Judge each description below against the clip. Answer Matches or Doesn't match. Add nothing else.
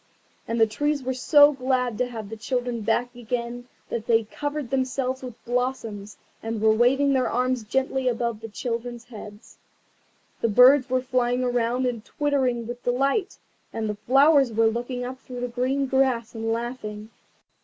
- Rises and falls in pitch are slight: Matches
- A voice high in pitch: Matches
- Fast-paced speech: Doesn't match